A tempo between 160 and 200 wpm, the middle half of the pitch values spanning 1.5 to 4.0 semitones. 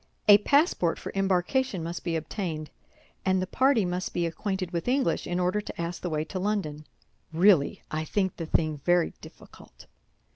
Yes: average, 175 wpm; average, 3.6 semitones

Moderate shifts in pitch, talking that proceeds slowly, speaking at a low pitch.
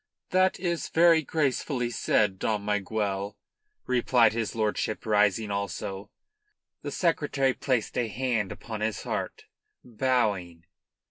Yes: average, 4.2 semitones; slow, 115 wpm; low, 110 Hz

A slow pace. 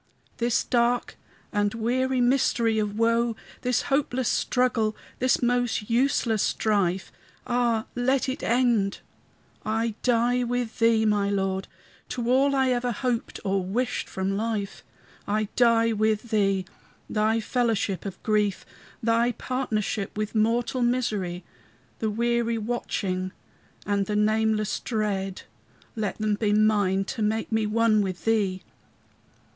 Yes: slow, 130 wpm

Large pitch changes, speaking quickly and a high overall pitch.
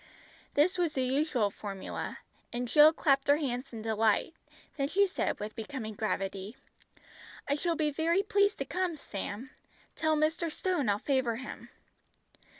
No: wide, 6.2 semitones; average, 150 wpm; very high, 275 Hz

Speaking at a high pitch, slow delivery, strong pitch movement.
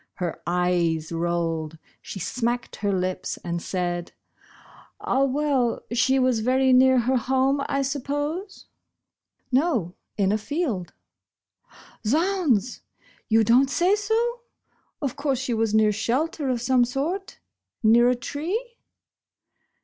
Yes: very high, 250 Hz; slow, 130 wpm; wide, 5.7 semitones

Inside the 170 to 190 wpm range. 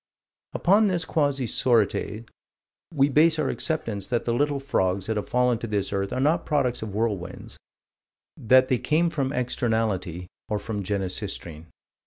No: average, 155 wpm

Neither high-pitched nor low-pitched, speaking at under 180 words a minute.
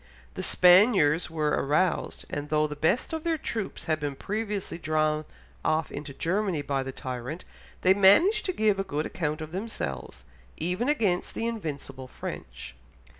Yes: medium, 165 Hz; average, 160 wpm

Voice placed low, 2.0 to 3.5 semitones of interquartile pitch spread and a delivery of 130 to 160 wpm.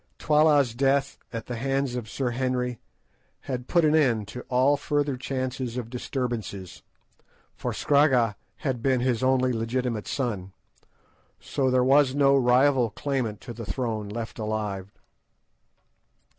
Yes: low, 125 Hz; average, 2.8 semitones; slow, 135 wpm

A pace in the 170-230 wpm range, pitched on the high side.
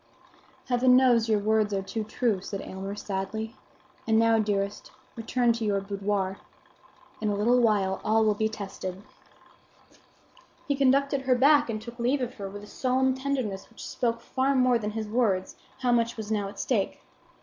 Yes: average, 175 wpm; high, 220 Hz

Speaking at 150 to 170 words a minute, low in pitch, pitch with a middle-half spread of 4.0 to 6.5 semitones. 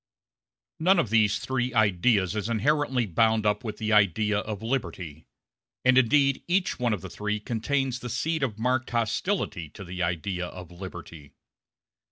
Yes: average, 160 wpm; low, 110 Hz; average, 4.6 semitones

